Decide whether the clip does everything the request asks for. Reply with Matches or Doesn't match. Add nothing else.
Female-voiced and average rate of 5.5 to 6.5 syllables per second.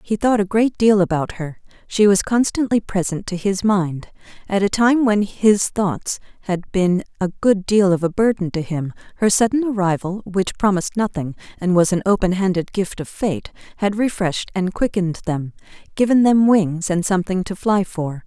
Doesn't match